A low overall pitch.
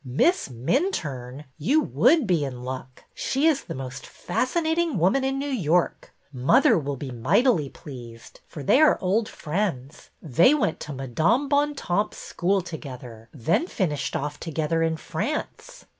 No: medium, 165 Hz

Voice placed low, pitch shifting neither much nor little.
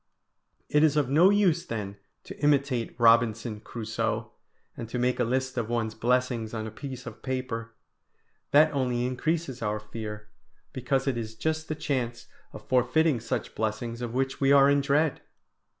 Yes: low, 125 Hz; average, 3.5 semitones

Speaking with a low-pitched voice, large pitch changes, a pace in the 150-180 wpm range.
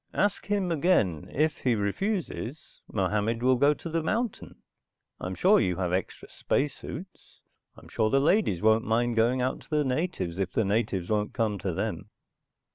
Yes: low, 120 Hz; wide, 7.6 semitones; average, 175 wpm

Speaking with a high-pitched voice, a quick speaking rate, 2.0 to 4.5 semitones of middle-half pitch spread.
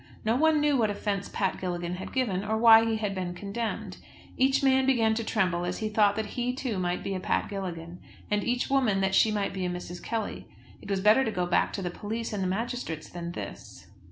Yes: high, 205 Hz; fast, 235 wpm; average, 3.8 semitones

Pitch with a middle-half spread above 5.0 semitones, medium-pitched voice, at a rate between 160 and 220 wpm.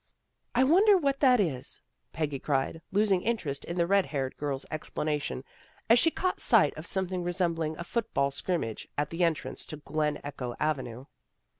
Yes: wide, 5.6 semitones; medium, 165 Hz; average, 170 wpm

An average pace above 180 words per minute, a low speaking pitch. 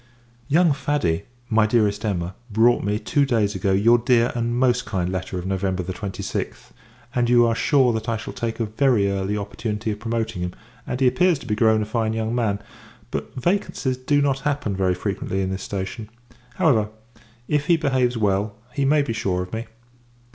Yes: average, 190 wpm; low, 110 Hz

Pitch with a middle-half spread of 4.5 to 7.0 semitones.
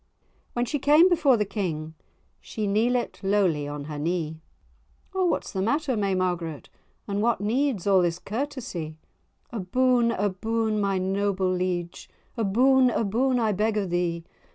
Yes: average, 5.0 semitones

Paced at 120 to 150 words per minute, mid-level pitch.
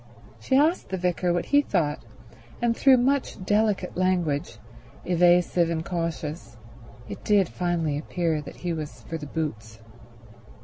Yes: average, 140 wpm; medium, 175 Hz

